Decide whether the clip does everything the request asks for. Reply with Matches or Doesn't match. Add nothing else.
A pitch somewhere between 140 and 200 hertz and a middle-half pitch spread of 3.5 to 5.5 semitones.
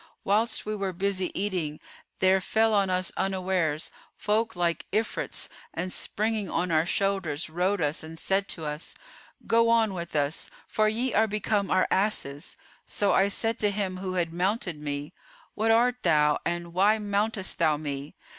Matches